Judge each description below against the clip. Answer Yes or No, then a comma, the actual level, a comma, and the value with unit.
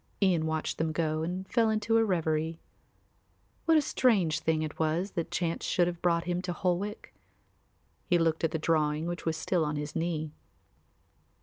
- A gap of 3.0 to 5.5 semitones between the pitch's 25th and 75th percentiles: No, narrow, 2.4 semitones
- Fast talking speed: No, average, 185 wpm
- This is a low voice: No, medium, 170 Hz